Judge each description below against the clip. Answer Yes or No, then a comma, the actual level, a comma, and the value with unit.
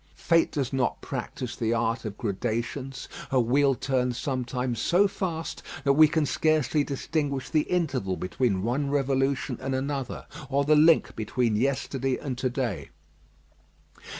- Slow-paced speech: No, average, 145 wpm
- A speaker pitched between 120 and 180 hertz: Yes, low, 135 Hz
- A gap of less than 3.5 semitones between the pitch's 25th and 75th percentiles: Yes, average, 2.9 semitones